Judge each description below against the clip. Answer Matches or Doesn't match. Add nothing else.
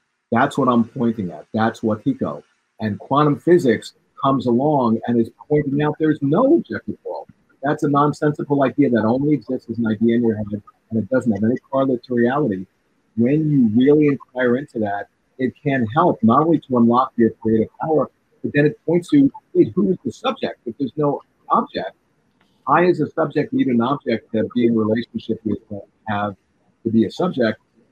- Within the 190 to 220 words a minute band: Matches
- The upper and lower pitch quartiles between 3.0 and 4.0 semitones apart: Doesn't match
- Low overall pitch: Matches